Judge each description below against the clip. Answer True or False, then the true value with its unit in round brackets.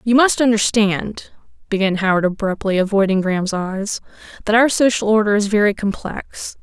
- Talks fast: False (145 wpm)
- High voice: True (205 Hz)